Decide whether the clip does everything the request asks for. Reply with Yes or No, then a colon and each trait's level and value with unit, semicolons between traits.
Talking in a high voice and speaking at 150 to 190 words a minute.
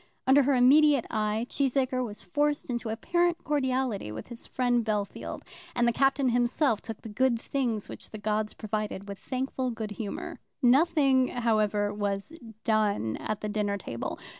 Yes: high, 235 Hz; average, 160 wpm